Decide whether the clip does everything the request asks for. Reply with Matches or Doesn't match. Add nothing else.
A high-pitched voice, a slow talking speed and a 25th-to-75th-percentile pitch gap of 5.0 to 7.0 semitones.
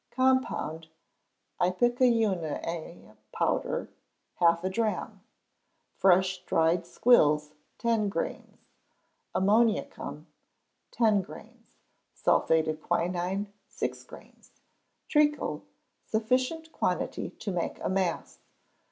Matches